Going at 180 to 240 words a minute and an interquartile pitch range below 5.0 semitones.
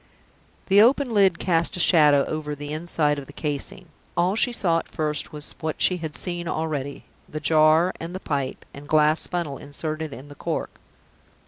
Yes: average, 185 wpm; average, 2.9 semitones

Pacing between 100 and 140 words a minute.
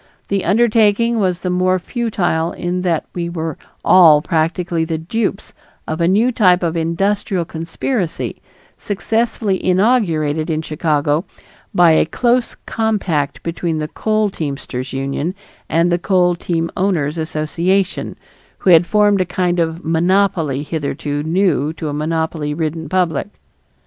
Yes: slow, 135 wpm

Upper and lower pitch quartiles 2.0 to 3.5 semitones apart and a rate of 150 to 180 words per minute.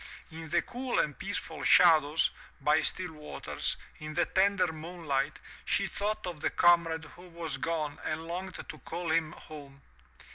Yes: narrow, 2.6 semitones; average, 155 wpm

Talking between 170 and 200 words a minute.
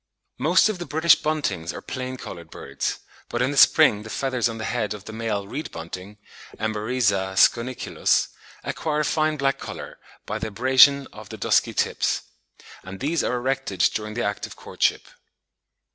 Yes: average, 175 wpm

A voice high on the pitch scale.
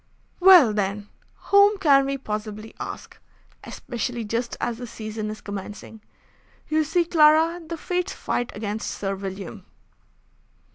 Yes: high, 235 Hz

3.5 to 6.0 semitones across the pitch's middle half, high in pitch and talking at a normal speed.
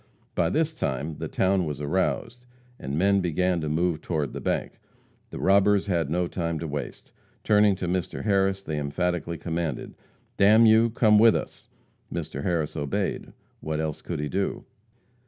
No: average, 4.2 semitones; very low, 90 Hz; average, 170 wpm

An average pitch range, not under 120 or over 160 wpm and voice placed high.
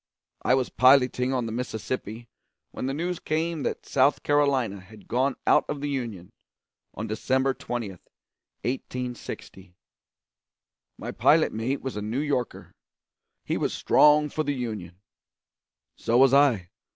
No: average, 3.9 semitones; average, 140 wpm; low, 125 Hz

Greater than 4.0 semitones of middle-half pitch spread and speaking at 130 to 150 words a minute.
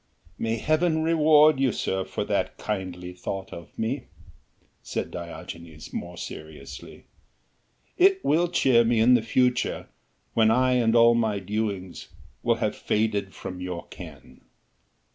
Yes: wide, 5.6 semitones; slow, 135 wpm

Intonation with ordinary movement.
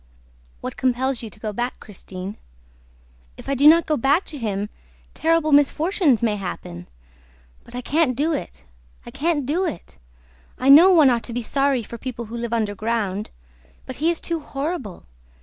No: wide, 5.7 semitones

